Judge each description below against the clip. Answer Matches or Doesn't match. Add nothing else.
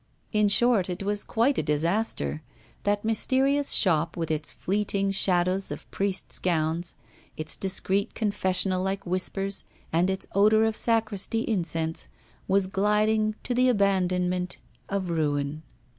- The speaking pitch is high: Matches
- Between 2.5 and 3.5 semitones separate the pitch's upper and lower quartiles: Matches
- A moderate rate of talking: Doesn't match